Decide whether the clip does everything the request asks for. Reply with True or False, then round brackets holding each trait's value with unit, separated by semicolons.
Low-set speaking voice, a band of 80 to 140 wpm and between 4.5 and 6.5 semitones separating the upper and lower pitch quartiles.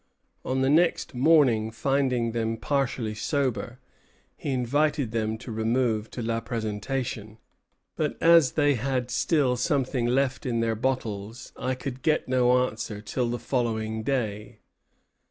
False (125 Hz; 135 wpm; 3.2 semitones)